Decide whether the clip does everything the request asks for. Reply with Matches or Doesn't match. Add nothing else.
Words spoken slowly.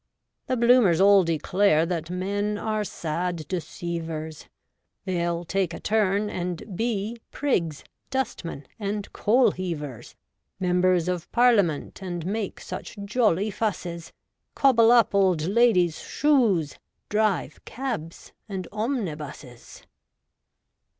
Matches